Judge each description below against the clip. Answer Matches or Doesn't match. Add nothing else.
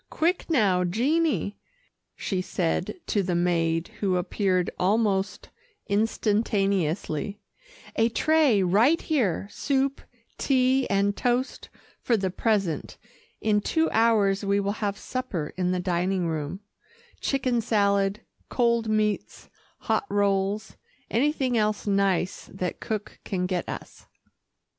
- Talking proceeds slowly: Matches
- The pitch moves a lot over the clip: Doesn't match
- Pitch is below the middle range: Doesn't match